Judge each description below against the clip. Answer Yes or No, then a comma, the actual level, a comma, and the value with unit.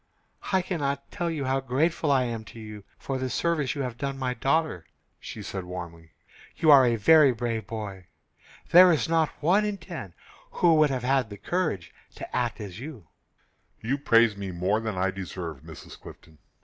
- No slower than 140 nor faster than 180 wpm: No, average, 190 wpm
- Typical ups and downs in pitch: No, wide, 7.1 semitones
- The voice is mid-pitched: No, low, 125 Hz